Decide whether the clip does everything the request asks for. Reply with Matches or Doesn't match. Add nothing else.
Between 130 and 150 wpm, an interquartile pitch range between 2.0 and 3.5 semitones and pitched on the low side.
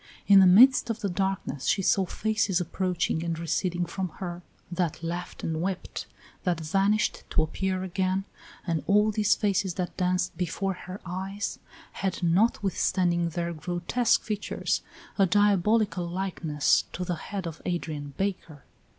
Doesn't match